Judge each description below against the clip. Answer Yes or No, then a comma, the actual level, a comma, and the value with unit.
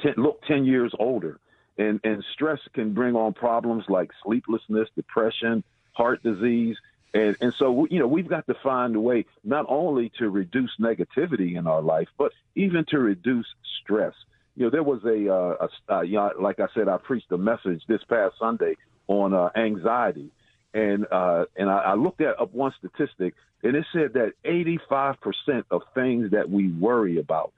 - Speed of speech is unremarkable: Yes, average, 190 wpm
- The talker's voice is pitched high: No, low, 115 Hz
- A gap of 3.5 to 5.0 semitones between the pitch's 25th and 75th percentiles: Yes, average, 3.9 semitones